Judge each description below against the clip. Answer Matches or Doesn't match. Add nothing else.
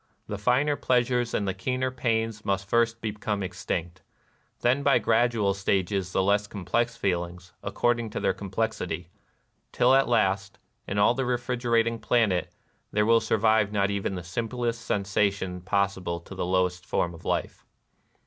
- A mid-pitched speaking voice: Doesn't match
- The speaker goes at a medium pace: Matches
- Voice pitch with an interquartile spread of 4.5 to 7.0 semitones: Doesn't match